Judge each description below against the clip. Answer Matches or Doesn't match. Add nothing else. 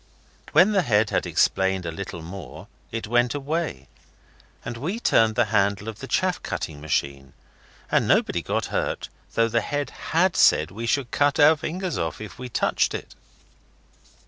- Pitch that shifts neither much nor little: Doesn't match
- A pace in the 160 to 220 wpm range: Matches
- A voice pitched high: Doesn't match